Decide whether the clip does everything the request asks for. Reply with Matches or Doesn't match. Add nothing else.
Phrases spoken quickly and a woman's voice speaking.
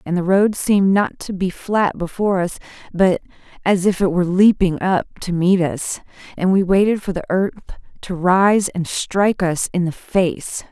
Doesn't match